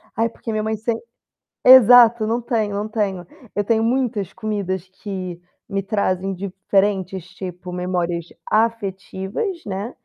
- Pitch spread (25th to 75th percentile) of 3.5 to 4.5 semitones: No, average, 3.1 semitones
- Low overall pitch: No, high, 205 Hz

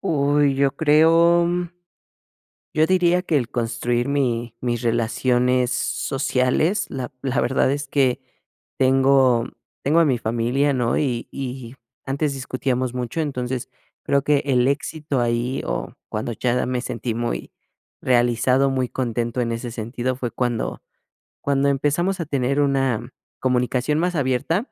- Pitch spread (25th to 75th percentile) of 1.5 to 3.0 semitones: Yes, average, 2.7 semitones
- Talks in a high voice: No, low, 130 Hz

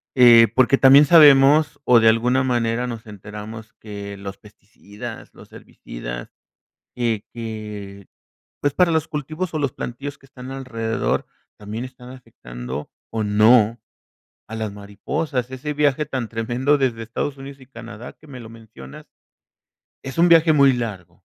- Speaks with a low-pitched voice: Yes, low, 120 Hz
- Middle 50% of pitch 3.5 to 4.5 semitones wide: Yes, average, 4.0 semitones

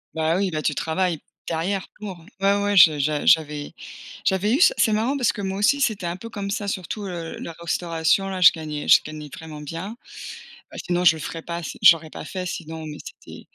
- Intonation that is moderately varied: Yes, average, 3.8 semitones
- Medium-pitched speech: Yes, medium, 175 Hz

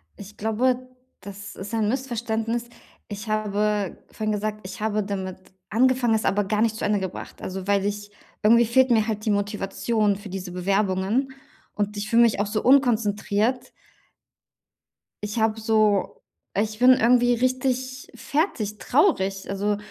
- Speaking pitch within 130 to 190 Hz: No, high, 215 Hz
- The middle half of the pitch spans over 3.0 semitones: No, average, 2.7 semitones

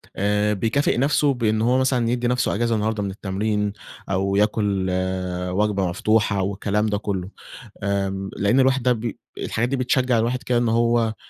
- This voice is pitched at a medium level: No, low, 110 Hz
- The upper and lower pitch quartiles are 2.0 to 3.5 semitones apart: Yes, average, 3.2 semitones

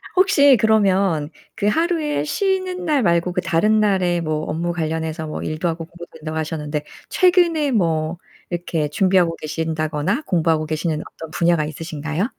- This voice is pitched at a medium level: Yes, medium, 170 Hz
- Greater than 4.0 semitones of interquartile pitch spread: Yes, average, 5.3 semitones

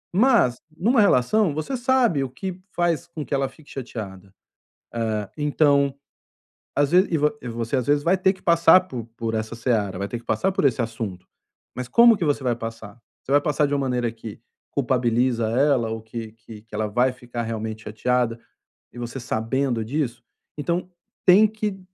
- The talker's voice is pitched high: No, low, 125 Hz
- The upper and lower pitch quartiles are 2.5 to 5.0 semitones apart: No, wide, 5.6 semitones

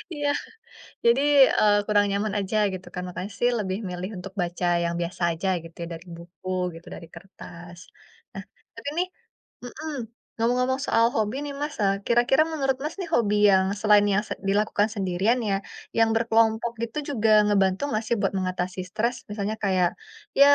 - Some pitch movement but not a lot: Yes, average, 4.0 semitones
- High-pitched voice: Yes, high, 205 Hz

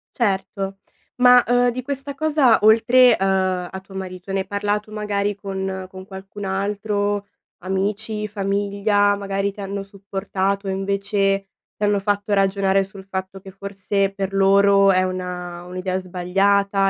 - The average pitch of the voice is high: Yes, high, 195 Hz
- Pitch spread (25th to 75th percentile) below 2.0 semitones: Yes, narrow, 1.2 semitones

